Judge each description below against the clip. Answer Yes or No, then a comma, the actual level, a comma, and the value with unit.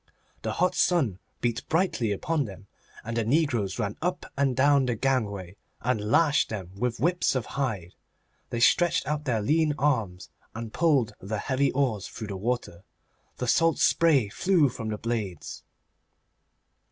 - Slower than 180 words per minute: Yes, average, 155 wpm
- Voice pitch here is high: No, low, 120 Hz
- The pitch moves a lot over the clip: Yes, wide, 5.8 semitones